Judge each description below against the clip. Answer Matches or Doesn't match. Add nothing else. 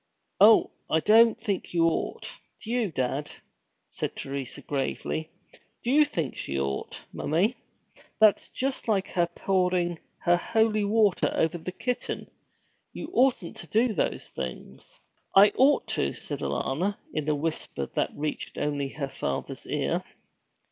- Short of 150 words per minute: Matches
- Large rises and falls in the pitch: Matches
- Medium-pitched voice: Matches